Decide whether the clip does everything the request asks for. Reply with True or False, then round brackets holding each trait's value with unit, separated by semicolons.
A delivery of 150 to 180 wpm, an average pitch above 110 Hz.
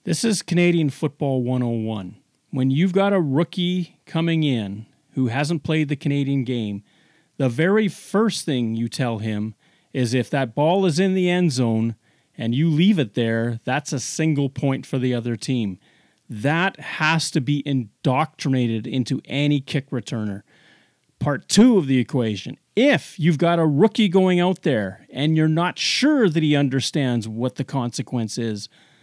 True (165 wpm; 140 Hz)